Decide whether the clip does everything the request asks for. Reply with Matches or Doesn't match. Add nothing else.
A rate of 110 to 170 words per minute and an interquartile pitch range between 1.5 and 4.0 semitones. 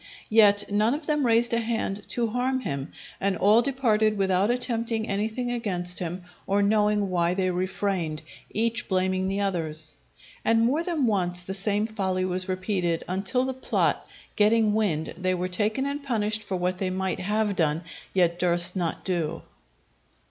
Matches